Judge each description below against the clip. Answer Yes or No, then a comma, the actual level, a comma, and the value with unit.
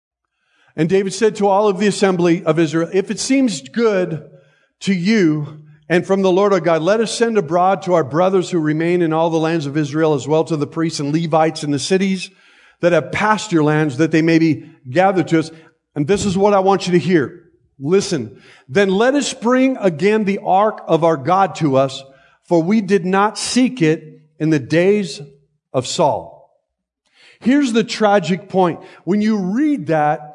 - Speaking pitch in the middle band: Yes, medium, 175 Hz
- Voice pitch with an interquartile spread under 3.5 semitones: No, average, 4.1 semitones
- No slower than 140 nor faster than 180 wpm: No, average, 200 wpm